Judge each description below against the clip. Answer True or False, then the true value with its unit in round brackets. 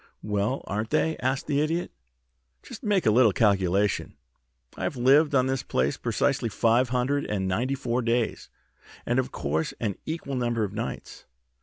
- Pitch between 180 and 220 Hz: False (120 Hz)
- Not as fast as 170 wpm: True (160 wpm)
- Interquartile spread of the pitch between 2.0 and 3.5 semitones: False (4.5 semitones)